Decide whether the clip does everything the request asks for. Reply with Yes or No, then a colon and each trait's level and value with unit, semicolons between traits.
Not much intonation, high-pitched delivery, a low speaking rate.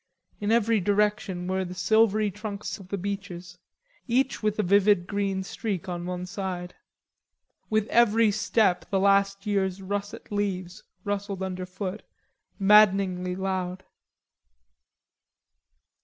Yes: narrow, 2.2 semitones; high, 195 Hz; slow, 115 wpm